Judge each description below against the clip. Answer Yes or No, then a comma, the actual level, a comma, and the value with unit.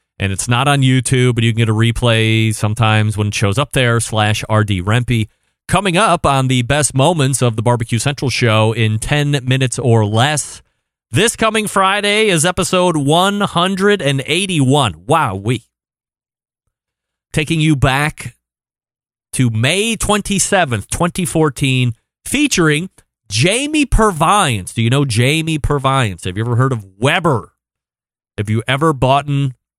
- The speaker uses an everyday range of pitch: No, wide, 5.9 semitones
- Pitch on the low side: Yes, low, 130 Hz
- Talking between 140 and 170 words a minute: Yes, average, 145 wpm